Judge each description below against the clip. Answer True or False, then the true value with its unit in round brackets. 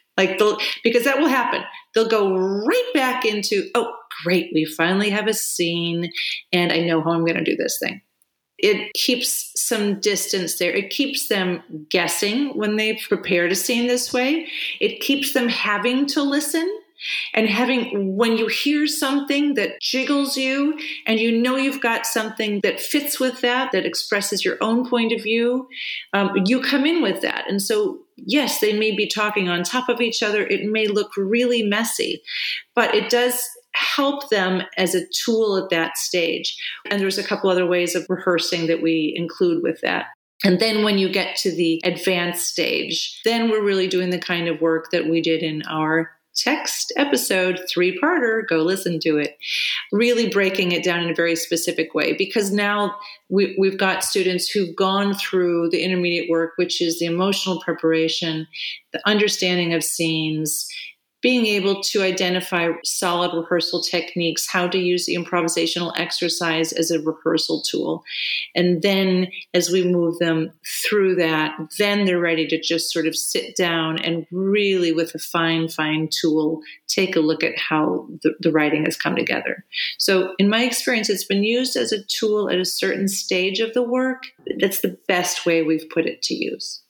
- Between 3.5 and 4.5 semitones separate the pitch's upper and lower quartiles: False (5.3 semitones)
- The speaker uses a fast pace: False (180 wpm)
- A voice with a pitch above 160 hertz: True (190 Hz)